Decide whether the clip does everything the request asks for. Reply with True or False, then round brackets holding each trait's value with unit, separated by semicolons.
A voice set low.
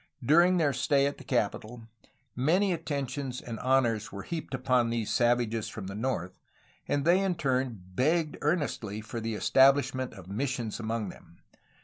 True (130 Hz)